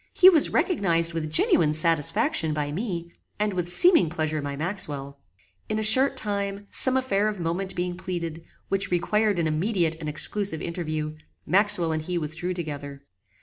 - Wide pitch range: No, average, 4.5 semitones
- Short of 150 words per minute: No, average, 160 wpm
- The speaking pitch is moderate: Yes, medium, 175 Hz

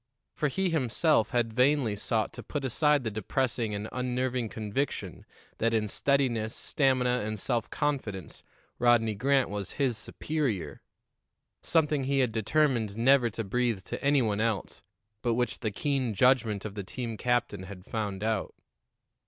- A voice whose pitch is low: Yes, low, 120 Hz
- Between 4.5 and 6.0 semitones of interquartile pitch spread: No, average, 3.8 semitones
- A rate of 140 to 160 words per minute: Yes, average, 155 wpm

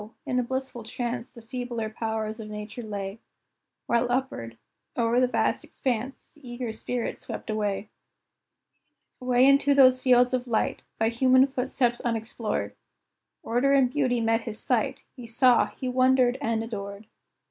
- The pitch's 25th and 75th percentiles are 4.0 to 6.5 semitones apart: No, narrow, 2.4 semitones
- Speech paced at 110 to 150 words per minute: Yes, average, 145 wpm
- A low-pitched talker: No, high, 240 Hz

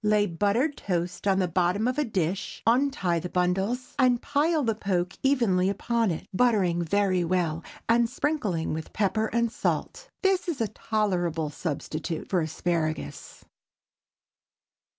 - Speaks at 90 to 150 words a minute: Yes, average, 140 wpm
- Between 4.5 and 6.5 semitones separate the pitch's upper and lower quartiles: Yes, average, 5.2 semitones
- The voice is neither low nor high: No, high, 200 Hz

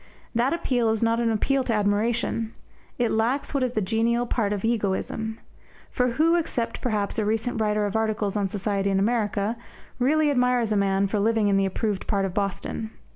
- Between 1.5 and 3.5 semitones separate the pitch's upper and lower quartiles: Yes, average, 2.7 semitones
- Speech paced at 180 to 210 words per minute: Yes, average, 190 wpm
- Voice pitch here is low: No, high, 220 Hz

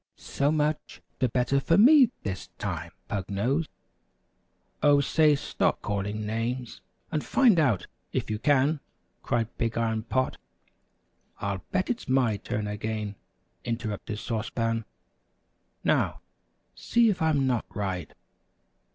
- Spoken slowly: Yes, slow, 125 wpm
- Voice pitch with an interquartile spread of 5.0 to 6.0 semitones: Yes, wide, 5.6 semitones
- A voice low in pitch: Yes, low, 120 Hz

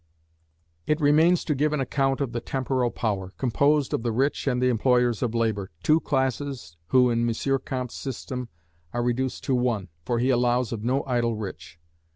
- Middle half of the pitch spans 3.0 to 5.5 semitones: No, narrow, 2.5 semitones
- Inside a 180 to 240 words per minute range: Yes, average, 185 wpm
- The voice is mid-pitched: No, low, 125 Hz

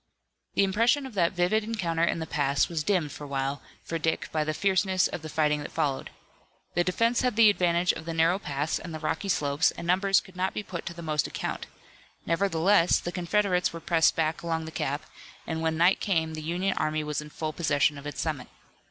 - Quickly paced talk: Yes, fast, 220 wpm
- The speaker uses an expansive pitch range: No, average, 3.4 semitones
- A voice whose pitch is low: No, medium, 165 Hz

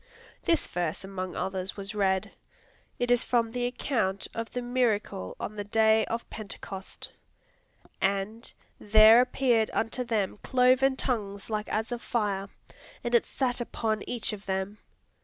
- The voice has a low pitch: No, high, 220 Hz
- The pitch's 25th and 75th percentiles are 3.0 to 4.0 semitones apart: Yes, average, 3.6 semitones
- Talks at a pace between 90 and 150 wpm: Yes, average, 145 wpm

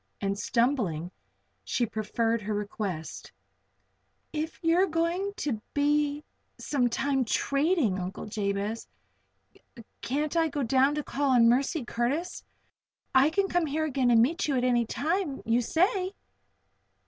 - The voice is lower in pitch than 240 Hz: No, very high, 270 Hz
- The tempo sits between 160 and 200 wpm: No, slow, 135 wpm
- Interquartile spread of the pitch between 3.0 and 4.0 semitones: No, wide, 5.5 semitones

